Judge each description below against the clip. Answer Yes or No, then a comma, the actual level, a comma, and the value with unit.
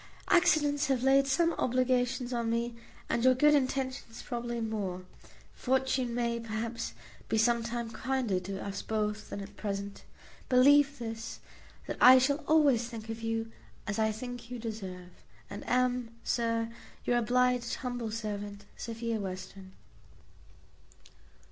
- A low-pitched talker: No, high, 235 Hz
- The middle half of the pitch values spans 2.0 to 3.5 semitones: Yes, average, 2.7 semitones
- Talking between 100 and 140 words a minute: Yes, slow, 135 wpm